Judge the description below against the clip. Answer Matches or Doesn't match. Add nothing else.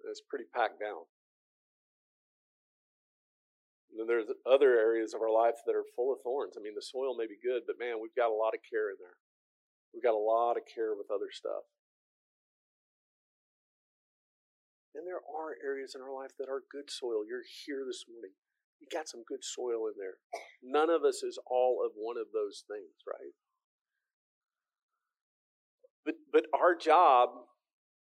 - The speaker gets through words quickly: Doesn't match